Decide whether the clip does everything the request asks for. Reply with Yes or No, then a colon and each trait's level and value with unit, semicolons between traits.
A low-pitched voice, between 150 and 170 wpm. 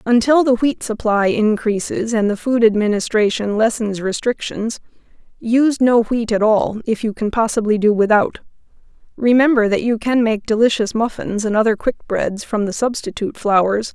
No: high, 220 Hz; average, 160 wpm